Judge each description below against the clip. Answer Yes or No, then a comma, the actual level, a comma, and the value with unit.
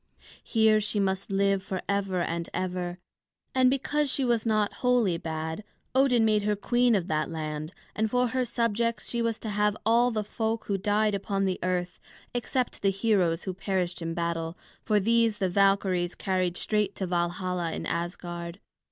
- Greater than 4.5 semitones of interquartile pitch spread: No, average, 4.0 semitones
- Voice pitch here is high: Yes, high, 200 Hz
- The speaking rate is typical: Yes, average, 170 wpm